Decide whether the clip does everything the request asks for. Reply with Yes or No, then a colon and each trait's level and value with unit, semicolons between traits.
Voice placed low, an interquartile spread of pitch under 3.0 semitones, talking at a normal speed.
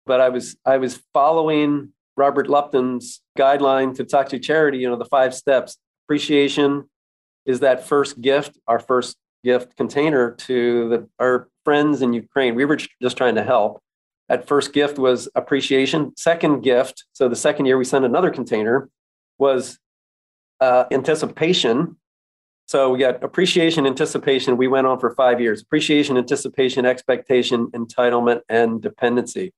Yes: low, 130 Hz; narrow, 2.5 semitones; average, 150 wpm